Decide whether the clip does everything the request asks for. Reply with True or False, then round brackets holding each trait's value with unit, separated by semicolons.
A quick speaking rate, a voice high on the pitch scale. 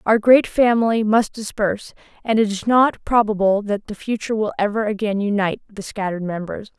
False (175 wpm; 205 Hz)